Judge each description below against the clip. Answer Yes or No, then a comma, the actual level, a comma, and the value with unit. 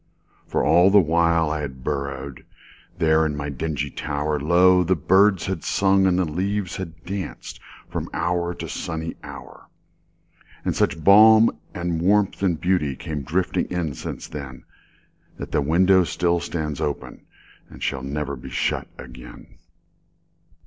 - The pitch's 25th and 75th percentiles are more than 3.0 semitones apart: Yes, average, 3.6 semitones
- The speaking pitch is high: No, very low, 85 Hz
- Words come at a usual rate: No, slow, 130 wpm